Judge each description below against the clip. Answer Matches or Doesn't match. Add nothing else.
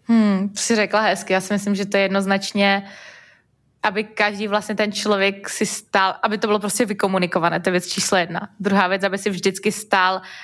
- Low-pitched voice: Doesn't match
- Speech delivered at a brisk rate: Matches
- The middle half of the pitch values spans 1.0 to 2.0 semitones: Matches